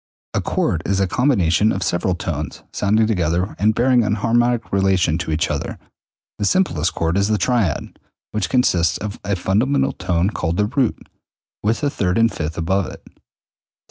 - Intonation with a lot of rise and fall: No, average, 4.6 semitones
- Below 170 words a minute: No, average, 175 wpm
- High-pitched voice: No, low, 100 Hz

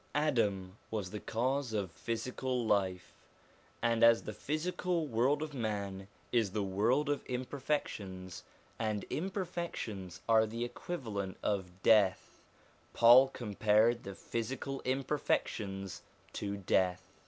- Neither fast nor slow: No, slow, 115 wpm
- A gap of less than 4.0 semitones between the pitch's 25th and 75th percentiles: No, average, 4.9 semitones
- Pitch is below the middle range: Yes, low, 110 Hz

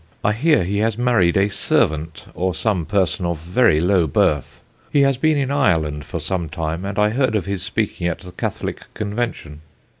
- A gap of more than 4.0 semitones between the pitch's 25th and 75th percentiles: Yes, average, 5.1 semitones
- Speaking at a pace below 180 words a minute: No, average, 190 wpm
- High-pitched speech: No, very low, 95 Hz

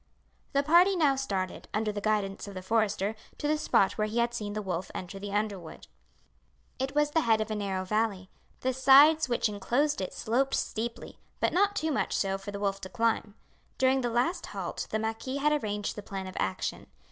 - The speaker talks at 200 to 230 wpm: Yes, fast, 205 wpm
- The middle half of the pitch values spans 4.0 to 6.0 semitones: Yes, average, 5.2 semitones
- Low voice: No, high, 220 Hz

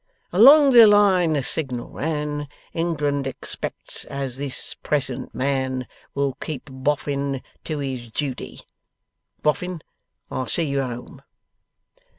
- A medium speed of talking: No, slow, 115 wpm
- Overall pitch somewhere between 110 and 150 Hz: Yes, medium, 140 Hz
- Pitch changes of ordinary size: Yes, average, 3.3 semitones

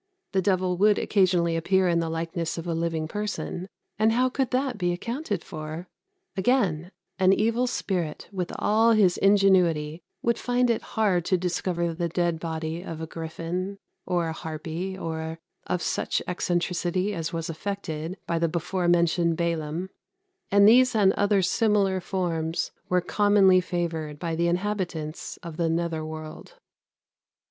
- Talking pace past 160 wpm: No, average, 155 wpm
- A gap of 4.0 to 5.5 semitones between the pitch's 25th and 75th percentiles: No, average, 3.1 semitones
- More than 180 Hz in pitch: No, medium, 175 Hz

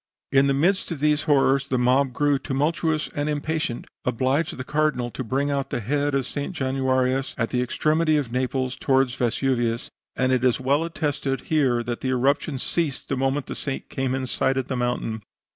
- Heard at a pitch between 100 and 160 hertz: Yes, low, 135 Hz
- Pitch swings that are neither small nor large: No, narrow, 2.3 semitones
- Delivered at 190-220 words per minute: Yes, average, 195 wpm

